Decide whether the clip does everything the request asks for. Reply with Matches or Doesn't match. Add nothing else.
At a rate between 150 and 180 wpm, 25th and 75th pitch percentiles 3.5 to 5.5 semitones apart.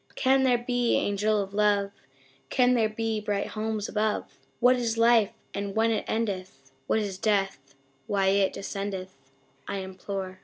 Doesn't match